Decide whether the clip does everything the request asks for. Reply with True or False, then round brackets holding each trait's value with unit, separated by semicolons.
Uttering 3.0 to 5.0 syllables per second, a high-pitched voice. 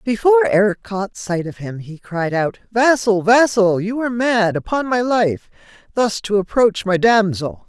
True (4.6 syllables/s; 210 Hz)